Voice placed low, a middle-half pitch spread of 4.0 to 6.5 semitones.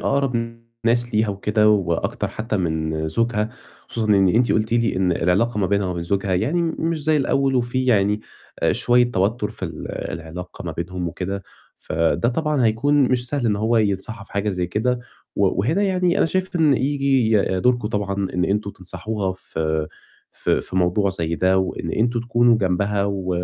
Yes: low, 105 Hz; average, 4.5 semitones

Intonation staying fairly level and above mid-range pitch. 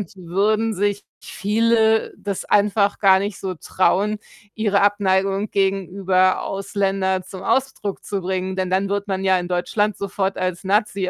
Yes: narrow, 1.5 semitones; high, 195 Hz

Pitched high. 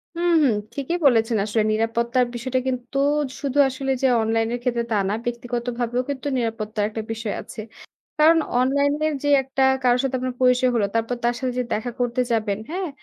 Yes: high, 245 Hz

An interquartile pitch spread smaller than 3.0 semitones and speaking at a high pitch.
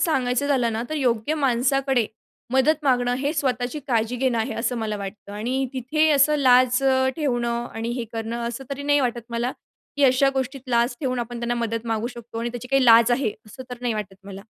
Yes: narrow, 2.6 semitones; high, 245 Hz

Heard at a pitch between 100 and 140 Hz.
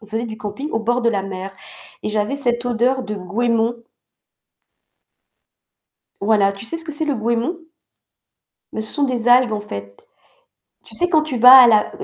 No: high, 230 Hz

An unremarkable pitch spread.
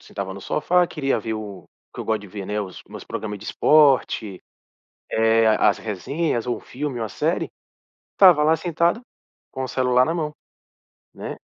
No: wide, 6.3 semitones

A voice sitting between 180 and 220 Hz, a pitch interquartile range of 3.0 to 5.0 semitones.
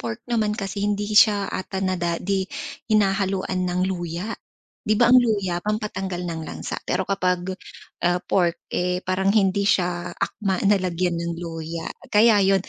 No: high, 190 Hz; narrow, 2.6 semitones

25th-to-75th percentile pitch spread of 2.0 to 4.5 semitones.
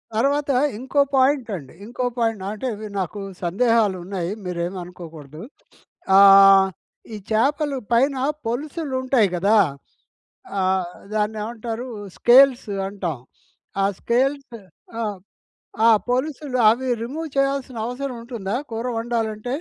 No: average, 4.9 semitones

